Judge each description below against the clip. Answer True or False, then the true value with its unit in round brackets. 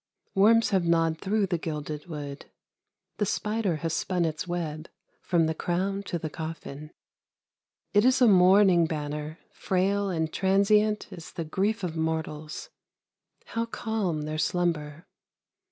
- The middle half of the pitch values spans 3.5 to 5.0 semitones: True (4.0 semitones)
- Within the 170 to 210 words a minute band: False (135 wpm)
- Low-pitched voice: False (175 Hz)